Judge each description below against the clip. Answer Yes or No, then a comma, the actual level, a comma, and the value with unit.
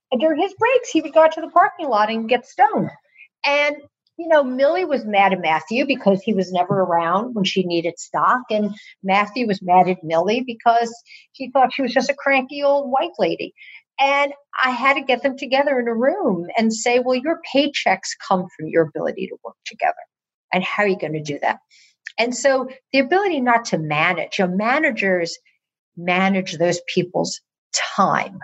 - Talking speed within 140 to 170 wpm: No, average, 195 wpm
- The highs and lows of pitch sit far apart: Yes, wide, 6.9 semitones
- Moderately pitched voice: No, high, 245 Hz